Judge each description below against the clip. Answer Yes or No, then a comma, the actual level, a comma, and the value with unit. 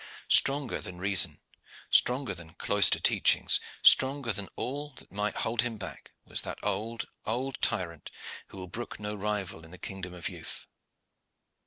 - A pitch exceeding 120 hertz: No, low, 105 Hz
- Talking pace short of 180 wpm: Yes, average, 155 wpm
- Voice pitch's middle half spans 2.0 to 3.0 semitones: No, average, 4.8 semitones